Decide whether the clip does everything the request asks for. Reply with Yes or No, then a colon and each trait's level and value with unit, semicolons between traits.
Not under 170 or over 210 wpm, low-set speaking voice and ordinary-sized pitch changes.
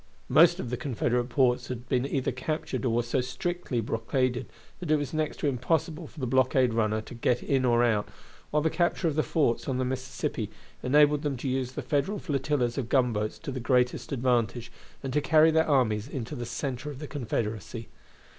Yes: average, 200 wpm; low, 130 Hz; average, 3.4 semitones